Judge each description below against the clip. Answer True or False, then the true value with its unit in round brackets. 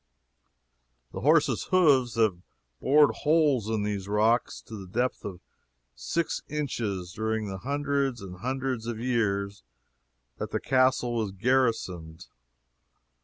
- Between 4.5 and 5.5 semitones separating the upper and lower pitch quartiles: True (4.8 semitones)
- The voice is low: True (115 Hz)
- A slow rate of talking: True (120 wpm)